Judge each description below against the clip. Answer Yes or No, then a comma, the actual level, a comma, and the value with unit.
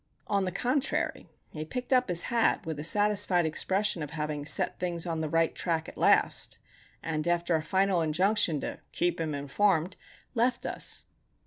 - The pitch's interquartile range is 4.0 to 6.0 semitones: Yes, average, 4.4 semitones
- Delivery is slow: No, average, 175 wpm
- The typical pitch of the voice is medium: Yes, medium, 175 Hz